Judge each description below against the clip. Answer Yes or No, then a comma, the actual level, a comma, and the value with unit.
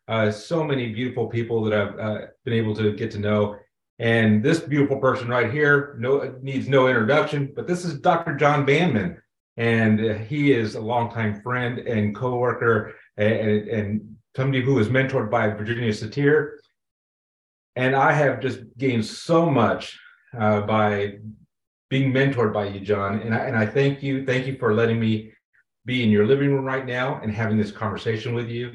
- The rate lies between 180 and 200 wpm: Yes, average, 185 wpm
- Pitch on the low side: Yes, low, 120 Hz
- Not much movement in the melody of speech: No, average, 3.8 semitones